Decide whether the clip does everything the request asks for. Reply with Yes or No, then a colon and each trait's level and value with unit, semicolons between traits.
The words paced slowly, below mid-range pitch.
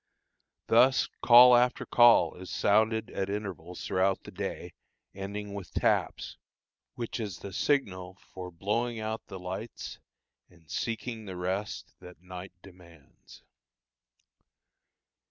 Yes: slow, 120 wpm; low, 100 Hz